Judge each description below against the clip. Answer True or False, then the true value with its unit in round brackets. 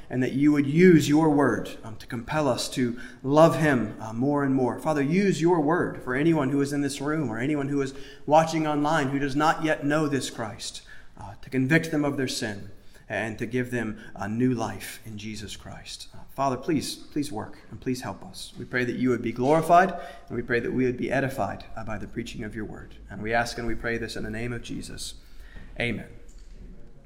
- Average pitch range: True (4.5 semitones)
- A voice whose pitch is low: True (130 Hz)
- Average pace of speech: False (230 wpm)